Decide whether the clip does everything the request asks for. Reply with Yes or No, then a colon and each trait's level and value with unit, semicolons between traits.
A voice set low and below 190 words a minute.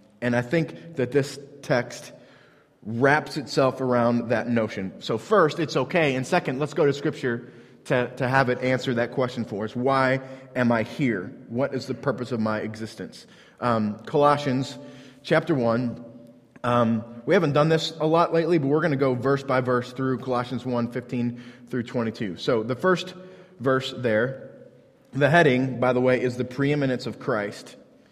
Yes: low, 130 Hz; average, 175 wpm